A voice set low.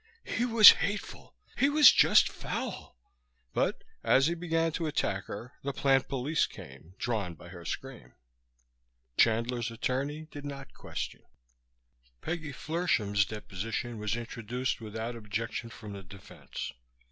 Yes: low, 120 Hz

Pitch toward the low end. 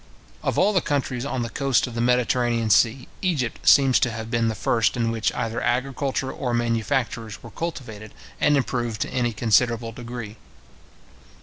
Yes: low, 120 Hz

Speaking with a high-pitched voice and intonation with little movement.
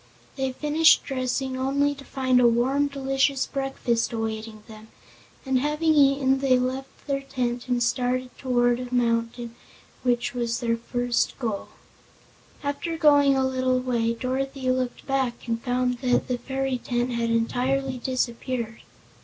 Yes: very high, 255 Hz; narrow, 2.0 semitones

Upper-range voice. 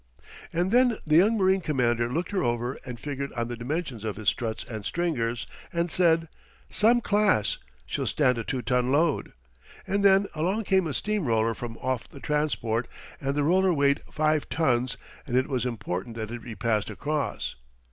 No: medium, 140 Hz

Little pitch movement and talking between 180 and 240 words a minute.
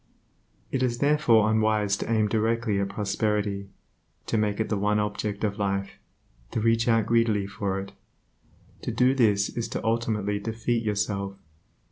No: narrow, 2.2 semitones; average, 155 wpm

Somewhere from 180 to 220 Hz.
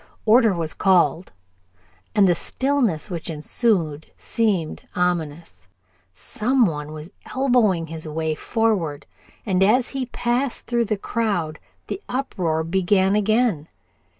Yes: high, 190 Hz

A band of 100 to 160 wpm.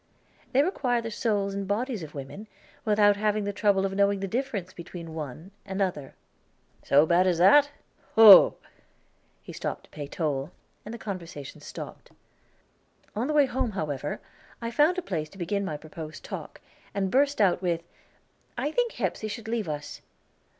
No: average, 170 wpm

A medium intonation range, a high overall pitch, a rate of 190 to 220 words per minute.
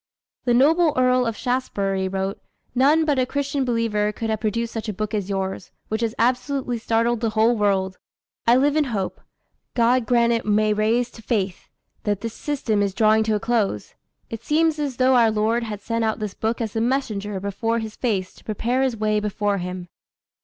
Yes: average, 3.0 semitones; high, 225 Hz; average, 200 wpm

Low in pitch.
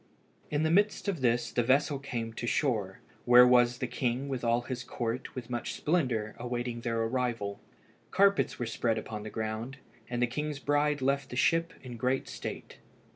Yes: low, 125 Hz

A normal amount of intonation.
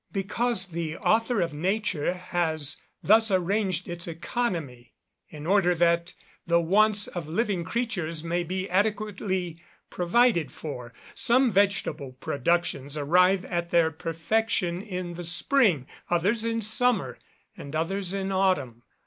Yes: average, 3.7 semitones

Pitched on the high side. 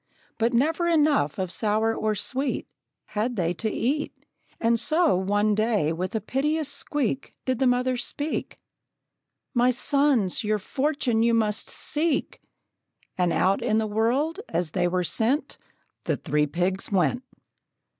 Yes: high, 230 Hz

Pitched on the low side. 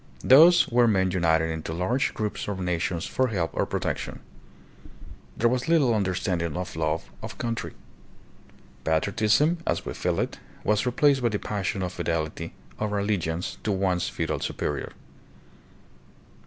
Yes: low, 100 Hz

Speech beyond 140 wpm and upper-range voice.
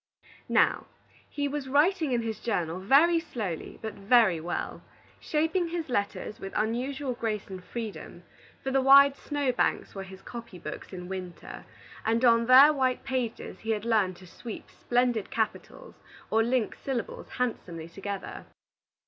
Yes: average, 150 wpm; high, 235 Hz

